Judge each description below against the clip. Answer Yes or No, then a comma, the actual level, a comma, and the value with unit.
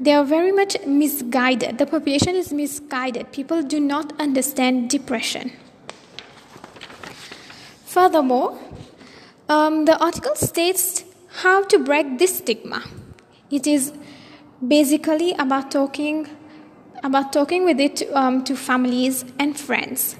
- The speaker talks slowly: Yes, slow, 115 wpm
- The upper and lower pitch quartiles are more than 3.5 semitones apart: No, average, 3.1 semitones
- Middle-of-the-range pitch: No, very high, 290 Hz